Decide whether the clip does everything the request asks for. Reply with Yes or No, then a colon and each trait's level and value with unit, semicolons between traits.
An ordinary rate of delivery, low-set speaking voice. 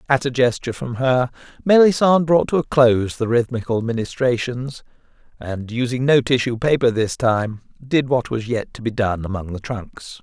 Yes: average, 165 wpm; low, 125 Hz